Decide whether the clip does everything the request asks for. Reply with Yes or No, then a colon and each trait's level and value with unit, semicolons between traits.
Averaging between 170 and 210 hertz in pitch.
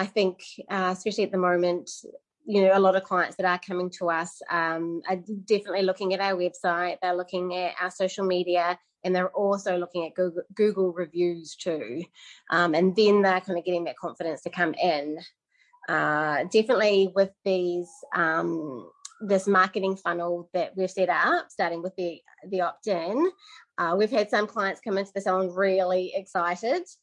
Yes: medium, 185 Hz